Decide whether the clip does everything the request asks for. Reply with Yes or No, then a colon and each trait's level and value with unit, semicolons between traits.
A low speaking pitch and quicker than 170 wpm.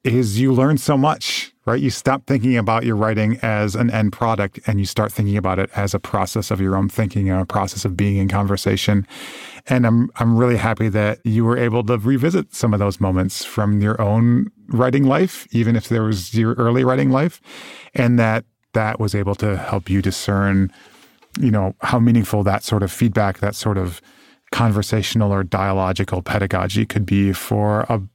Yes: low, 110 Hz; average, 195 wpm